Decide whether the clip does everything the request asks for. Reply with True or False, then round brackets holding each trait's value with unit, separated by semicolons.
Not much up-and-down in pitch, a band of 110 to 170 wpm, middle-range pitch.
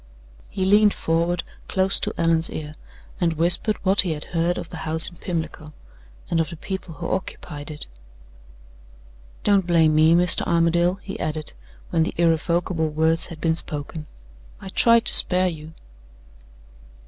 True (2.1 semitones; 155 wpm; 170 Hz)